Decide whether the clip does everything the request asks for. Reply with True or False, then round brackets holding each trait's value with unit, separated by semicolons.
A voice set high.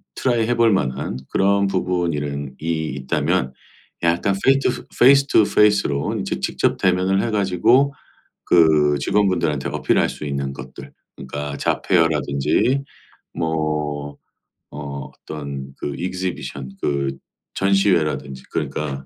False (80 Hz)